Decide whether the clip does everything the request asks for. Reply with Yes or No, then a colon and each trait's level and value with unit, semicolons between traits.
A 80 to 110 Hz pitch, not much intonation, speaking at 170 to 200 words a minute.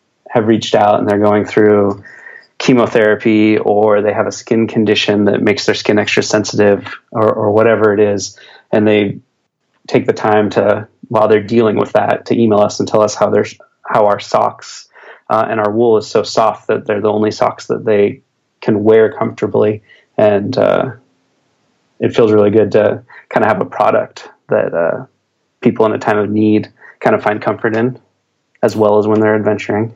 Yes: low, 105 Hz; narrow, 1.1 semitones; average, 190 wpm